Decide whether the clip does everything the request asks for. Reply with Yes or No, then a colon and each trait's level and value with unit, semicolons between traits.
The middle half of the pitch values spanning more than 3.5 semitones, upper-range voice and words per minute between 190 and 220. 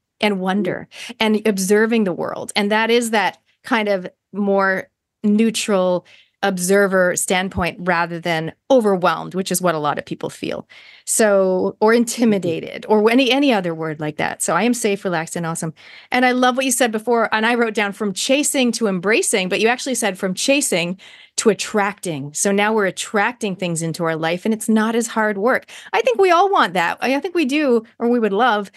Yes: average, 4.0 semitones; high, 210 Hz; average, 200 wpm